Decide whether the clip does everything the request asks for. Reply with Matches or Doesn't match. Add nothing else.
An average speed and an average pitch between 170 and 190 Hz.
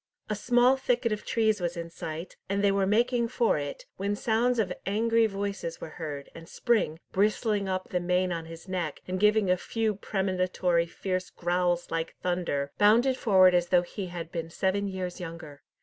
Matches